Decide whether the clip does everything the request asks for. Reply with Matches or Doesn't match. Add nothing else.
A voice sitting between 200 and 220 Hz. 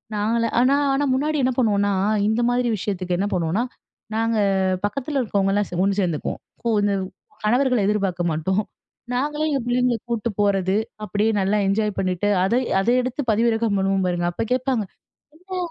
Matches